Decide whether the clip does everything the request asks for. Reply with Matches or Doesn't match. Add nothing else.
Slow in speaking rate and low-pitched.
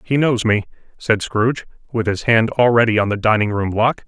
Doesn't match